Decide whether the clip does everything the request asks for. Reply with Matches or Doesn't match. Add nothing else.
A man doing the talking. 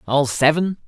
Matches